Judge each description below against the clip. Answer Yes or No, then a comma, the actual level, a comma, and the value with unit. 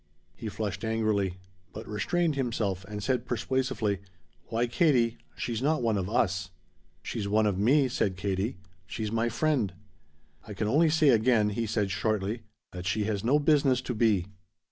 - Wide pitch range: No, average, 3.8 semitones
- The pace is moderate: Yes, average, 165 wpm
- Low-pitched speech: Yes, low, 110 Hz